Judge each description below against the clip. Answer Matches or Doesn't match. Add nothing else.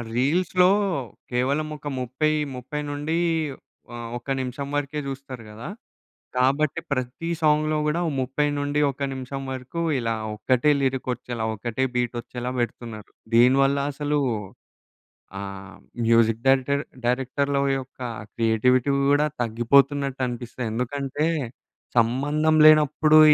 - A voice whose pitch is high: Doesn't match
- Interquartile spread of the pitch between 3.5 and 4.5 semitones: Doesn't match